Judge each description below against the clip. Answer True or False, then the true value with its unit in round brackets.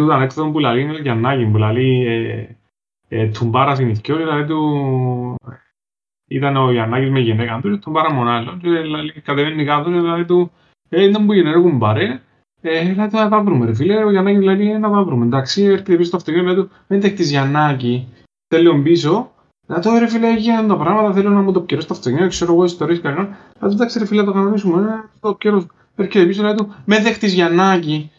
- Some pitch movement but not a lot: False (6.8 semitones)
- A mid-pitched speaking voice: True (170 Hz)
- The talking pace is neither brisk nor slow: False (65 wpm)